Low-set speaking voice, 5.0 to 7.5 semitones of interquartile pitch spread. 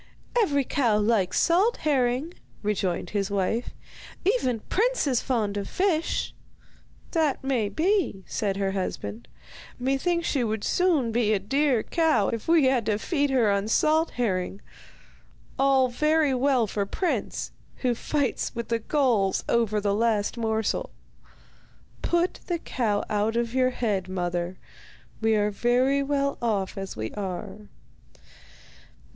No: high, 235 Hz; wide, 5.5 semitones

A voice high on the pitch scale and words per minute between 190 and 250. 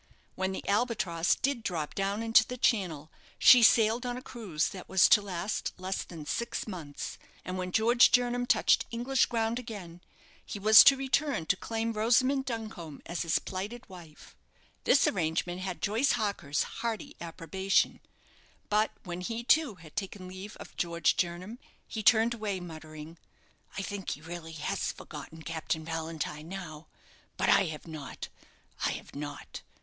No: high, 195 Hz; average, 160 wpm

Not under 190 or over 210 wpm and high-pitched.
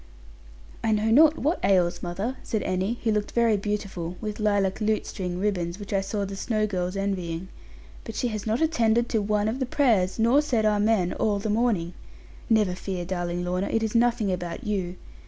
Yes: average, 195 wpm; high, 210 Hz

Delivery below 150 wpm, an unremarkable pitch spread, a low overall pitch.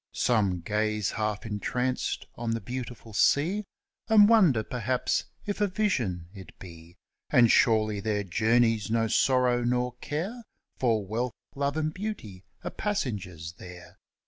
Yes: slow, 135 wpm; average, 4.8 semitones; low, 115 Hz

